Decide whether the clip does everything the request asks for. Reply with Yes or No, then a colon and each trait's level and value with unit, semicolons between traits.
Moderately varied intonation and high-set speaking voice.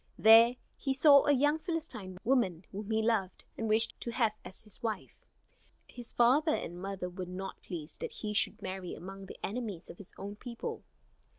Yes: average, 4.2 semitones; high, 215 Hz